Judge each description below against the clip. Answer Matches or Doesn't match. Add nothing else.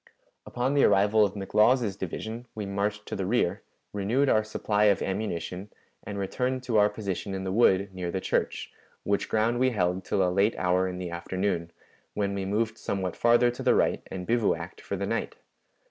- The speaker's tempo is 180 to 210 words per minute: Matches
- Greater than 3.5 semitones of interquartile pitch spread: Doesn't match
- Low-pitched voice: Matches